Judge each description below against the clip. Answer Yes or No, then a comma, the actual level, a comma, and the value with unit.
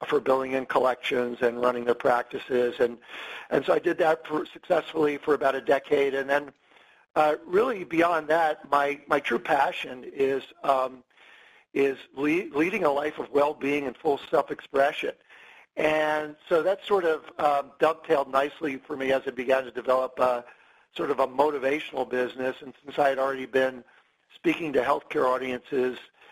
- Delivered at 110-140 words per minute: No, average, 165 wpm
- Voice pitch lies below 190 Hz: Yes, medium, 140 Hz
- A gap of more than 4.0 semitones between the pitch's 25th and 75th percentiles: No, average, 2.9 semitones